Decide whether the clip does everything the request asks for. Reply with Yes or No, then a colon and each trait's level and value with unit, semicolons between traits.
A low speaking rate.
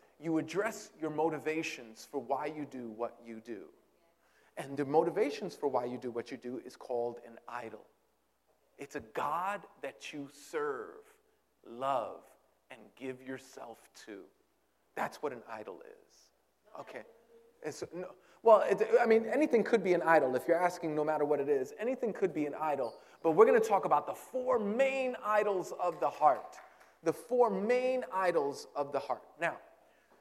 No: average, 175 wpm